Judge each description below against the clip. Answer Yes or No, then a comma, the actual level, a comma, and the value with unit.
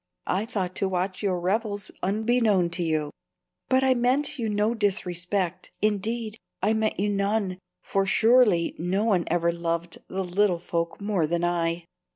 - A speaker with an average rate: Yes, average, 160 wpm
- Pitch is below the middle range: No, high, 195 Hz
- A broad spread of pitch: No, average, 3.7 semitones